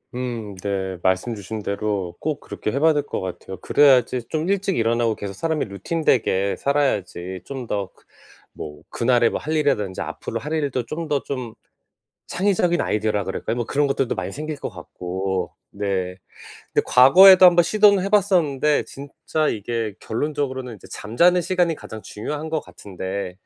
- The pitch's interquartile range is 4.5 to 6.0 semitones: No, wide, 7.4 semitones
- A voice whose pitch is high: No, low, 125 Hz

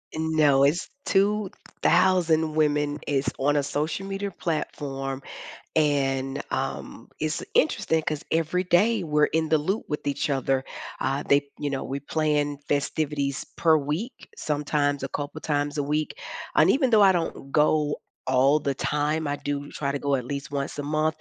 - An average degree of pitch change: No, narrow, 2.0 semitones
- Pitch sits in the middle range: Yes, medium, 150 Hz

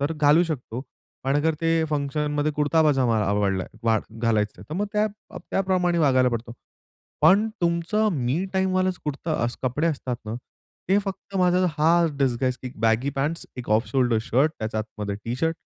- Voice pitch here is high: No, medium, 145 Hz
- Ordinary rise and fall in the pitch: No, wide, 5.9 semitones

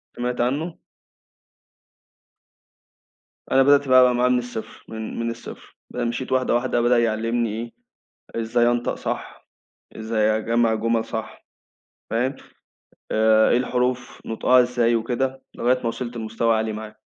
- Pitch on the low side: Yes, low, 120 Hz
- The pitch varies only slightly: Yes, narrow, 1.9 semitones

